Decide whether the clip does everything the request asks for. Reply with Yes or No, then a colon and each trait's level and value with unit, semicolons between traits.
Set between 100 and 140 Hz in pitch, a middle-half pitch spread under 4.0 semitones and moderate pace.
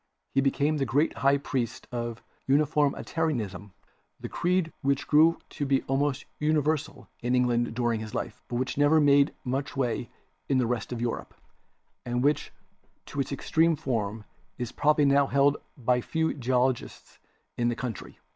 Yes: low, 135 Hz; average, 3.1 semitones; average, 165 wpm